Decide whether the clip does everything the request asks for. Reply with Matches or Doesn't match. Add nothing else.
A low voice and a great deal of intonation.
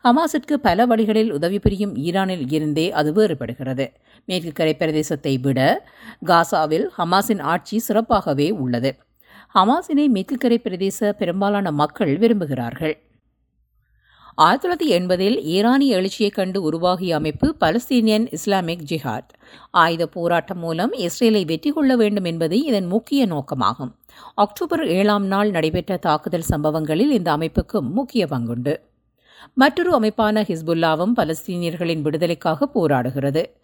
Doesn't match